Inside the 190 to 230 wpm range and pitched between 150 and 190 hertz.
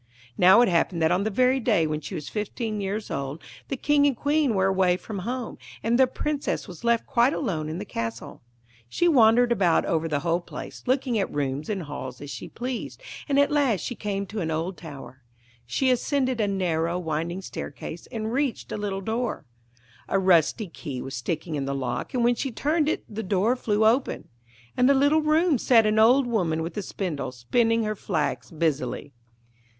No: average, 200 wpm; high, 205 Hz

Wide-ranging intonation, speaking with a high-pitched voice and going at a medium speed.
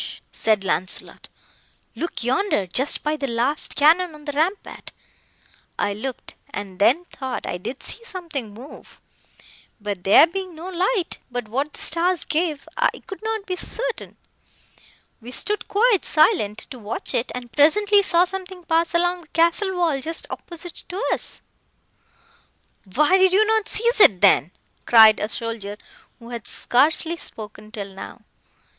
Yes: wide, 8.0 semitones; very high, 310 Hz; average, 150 wpm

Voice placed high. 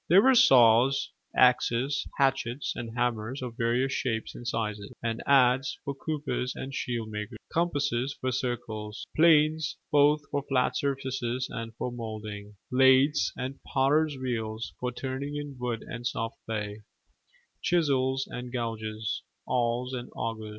No: low, 125 Hz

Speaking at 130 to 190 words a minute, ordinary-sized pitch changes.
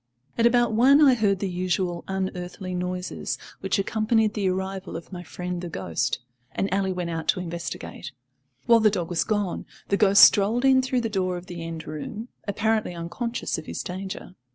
Yes: average, 185 wpm; average, 3.5 semitones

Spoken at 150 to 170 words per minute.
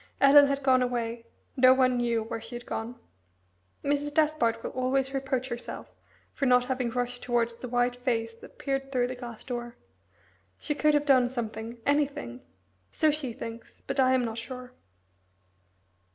Yes: average, 165 wpm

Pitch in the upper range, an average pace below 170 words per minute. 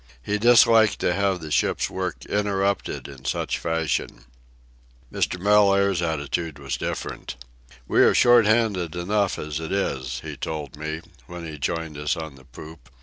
No: very low, 85 Hz; average, 155 wpm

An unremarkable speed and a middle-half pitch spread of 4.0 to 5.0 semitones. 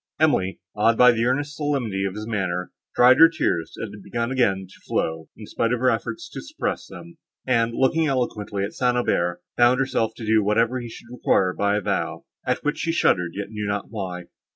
No: fast, 210 wpm; average, 4.3 semitones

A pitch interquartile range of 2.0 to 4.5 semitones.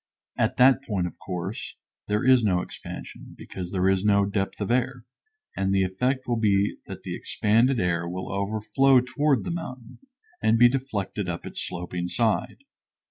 No: average, 5.0 semitones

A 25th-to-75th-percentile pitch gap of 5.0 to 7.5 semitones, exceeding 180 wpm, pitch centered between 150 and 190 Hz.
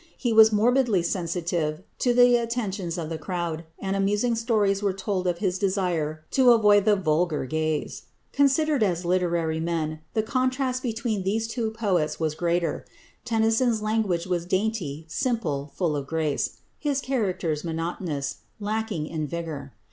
No: average, 5.3 semitones; average, 145 wpm; medium, 185 Hz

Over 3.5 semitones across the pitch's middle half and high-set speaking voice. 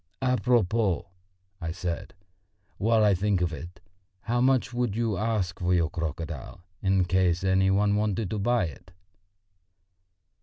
No: average, 4.1 semitones; very low, 95 Hz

